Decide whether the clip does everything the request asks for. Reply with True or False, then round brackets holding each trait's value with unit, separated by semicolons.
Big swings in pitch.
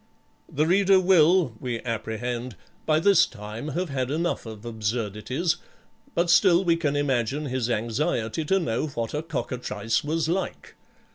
True (6.4 semitones)